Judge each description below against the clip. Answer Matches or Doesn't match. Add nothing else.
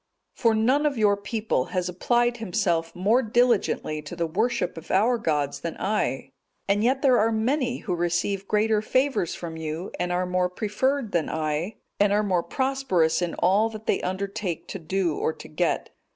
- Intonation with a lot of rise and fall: Doesn't match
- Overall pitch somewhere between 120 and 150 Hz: Doesn't match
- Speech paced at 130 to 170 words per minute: Doesn't match